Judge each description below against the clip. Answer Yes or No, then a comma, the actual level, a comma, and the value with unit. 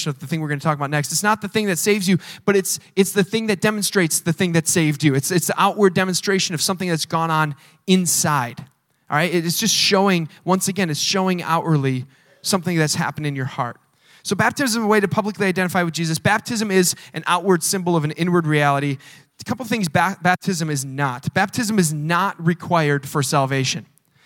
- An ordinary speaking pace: No, fast, 220 wpm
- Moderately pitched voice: Yes, medium, 170 Hz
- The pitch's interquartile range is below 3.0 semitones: No, average, 4.3 semitones